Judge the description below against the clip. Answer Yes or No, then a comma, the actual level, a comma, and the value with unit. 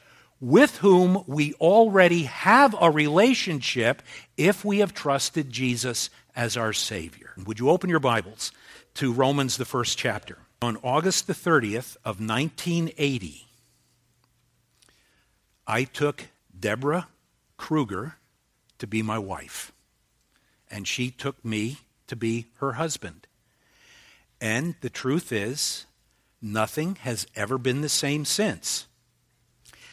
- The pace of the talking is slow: Yes, slow, 115 wpm